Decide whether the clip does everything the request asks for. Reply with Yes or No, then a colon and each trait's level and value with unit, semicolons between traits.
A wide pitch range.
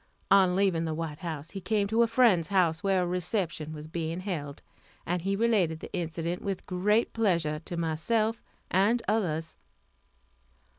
No: average, 3.7 semitones